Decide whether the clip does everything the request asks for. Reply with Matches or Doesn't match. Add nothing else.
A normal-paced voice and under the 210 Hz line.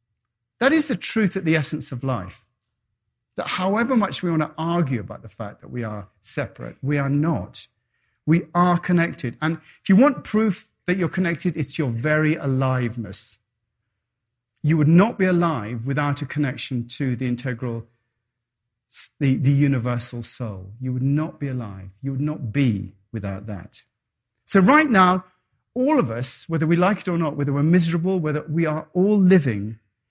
Matches